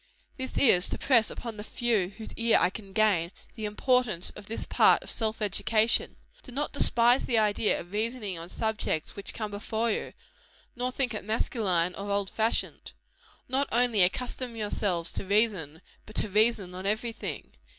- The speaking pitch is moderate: No, high, 215 Hz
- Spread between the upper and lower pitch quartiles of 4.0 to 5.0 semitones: No, average, 3.0 semitones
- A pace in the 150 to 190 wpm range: Yes, average, 175 wpm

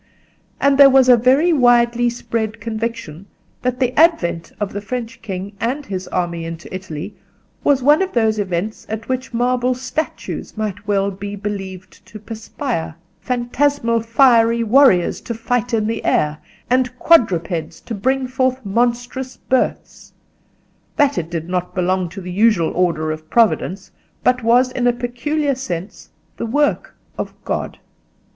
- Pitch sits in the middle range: No, high, 230 Hz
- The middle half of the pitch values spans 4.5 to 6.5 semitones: Yes, average, 4.9 semitones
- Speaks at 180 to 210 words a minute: No, average, 150 wpm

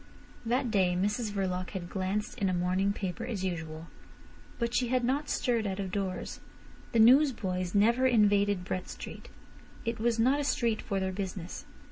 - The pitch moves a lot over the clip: No, average, 4.1 semitones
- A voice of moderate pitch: No, high, 205 Hz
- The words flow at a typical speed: Yes, average, 170 wpm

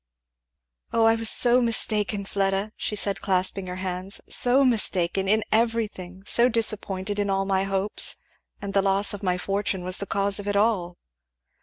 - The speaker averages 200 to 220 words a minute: No, average, 170 wpm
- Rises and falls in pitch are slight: Yes, narrow, 2.1 semitones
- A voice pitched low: No, high, 200 Hz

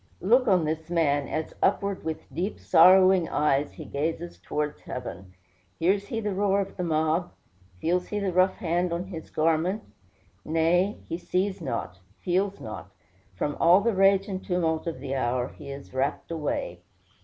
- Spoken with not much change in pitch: No, average, 3.9 semitones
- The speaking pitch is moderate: Yes, medium, 170 Hz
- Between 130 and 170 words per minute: Yes, average, 165 wpm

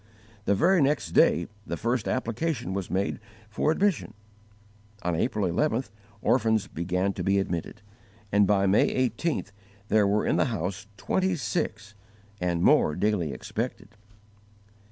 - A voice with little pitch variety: No, average, 5.0 semitones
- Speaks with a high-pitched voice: No, low, 105 Hz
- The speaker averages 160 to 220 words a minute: No, slow, 135 wpm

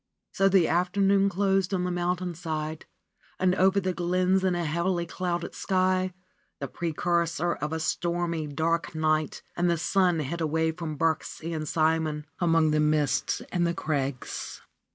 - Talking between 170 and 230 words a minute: No, average, 155 wpm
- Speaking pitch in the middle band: Yes, medium, 170 Hz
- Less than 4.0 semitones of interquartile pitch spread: Yes, narrow, 2.5 semitones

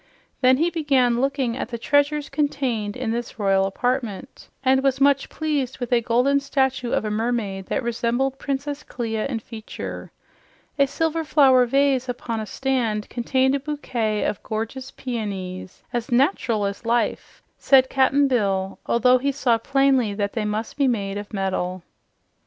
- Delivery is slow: No, average, 160 wpm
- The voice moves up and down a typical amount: Yes, average, 3.8 semitones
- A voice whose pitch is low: No, high, 245 Hz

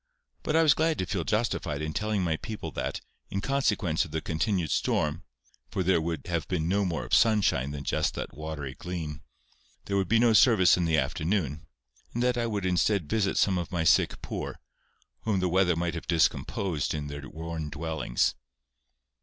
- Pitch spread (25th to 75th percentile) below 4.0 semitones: No, average, 4.5 semitones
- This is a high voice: No, very low, 85 Hz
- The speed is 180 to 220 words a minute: Yes, average, 185 wpm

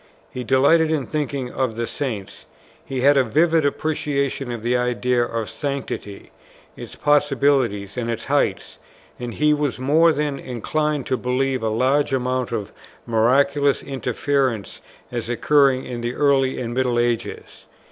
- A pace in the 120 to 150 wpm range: Yes, average, 145 wpm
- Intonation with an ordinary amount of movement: Yes, average, 3.0 semitones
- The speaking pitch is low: Yes, low, 130 Hz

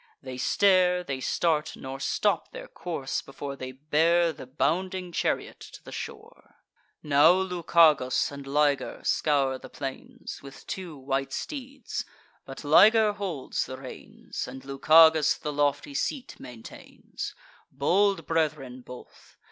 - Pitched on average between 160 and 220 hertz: No, medium, 150 Hz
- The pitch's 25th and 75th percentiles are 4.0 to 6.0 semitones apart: Yes, average, 4.8 semitones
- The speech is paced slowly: Yes, slow, 130 wpm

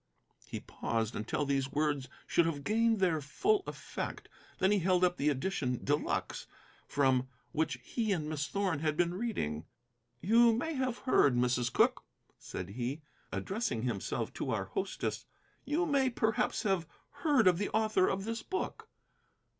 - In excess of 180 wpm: No, average, 160 wpm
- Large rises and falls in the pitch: Yes, wide, 8.2 semitones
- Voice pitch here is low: No, medium, 175 Hz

